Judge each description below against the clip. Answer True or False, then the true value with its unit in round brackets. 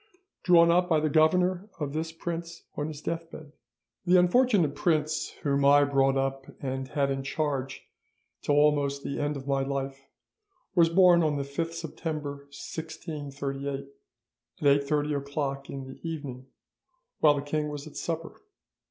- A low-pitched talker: False (145 Hz)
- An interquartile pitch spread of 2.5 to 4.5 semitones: True (2.9 semitones)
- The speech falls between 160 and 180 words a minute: False (150 wpm)